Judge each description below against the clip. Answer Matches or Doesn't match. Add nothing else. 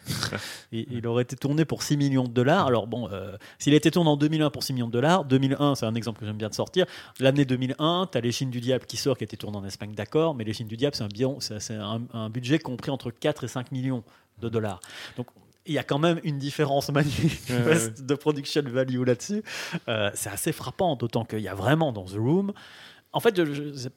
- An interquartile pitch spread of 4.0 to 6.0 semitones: Matches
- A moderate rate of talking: Doesn't match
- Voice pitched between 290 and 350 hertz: Doesn't match